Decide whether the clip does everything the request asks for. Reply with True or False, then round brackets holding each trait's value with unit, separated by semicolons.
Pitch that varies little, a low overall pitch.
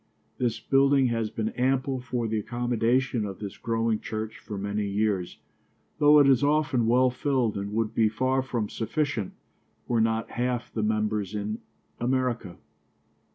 False (3.1 semitones; 115 Hz)